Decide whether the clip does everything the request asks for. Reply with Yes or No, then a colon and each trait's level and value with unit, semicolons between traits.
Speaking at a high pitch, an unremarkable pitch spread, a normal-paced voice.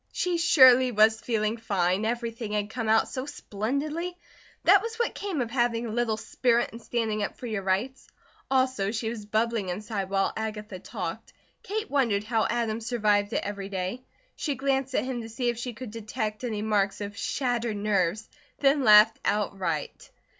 Yes: high, 225 Hz; average, 3.1 semitones; average, 175 wpm